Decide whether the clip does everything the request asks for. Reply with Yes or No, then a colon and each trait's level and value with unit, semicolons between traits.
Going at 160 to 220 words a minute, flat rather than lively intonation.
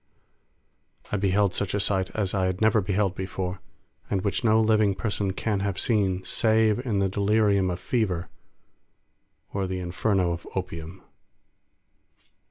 No: average, 145 wpm; narrow, 2.3 semitones